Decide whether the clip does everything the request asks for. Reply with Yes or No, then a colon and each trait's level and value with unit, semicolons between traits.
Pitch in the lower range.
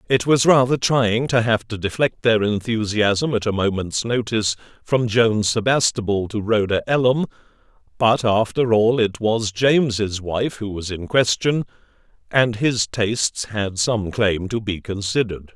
Yes: low, 110 Hz